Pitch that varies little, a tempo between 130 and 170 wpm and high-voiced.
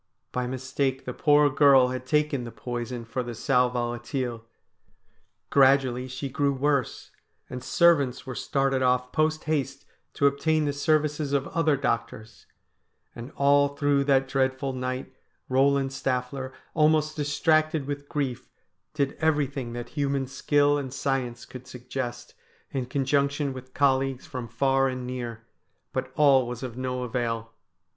No: narrow, 2.2 semitones; average, 140 wpm; low, 135 Hz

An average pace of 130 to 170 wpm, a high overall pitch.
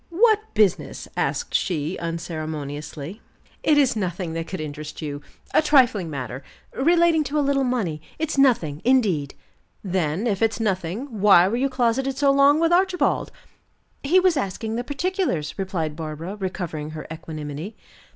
Yes: average, 150 wpm; high, 195 Hz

